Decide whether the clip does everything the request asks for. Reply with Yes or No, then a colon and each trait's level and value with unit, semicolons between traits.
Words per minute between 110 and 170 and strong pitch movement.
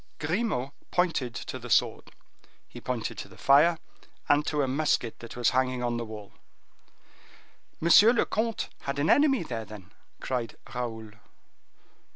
Yes: average, 150 wpm; wide, 5.7 semitones